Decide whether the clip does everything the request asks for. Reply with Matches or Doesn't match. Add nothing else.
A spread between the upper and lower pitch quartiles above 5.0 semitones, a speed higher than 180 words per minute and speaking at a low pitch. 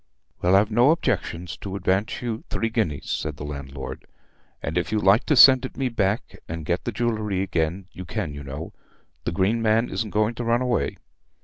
Matches